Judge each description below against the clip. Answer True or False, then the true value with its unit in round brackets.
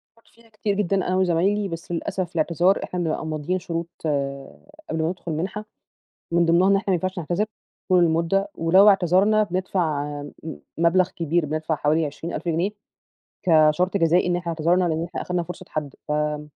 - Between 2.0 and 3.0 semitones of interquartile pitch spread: True (2.6 semitones)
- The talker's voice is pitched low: False (175 Hz)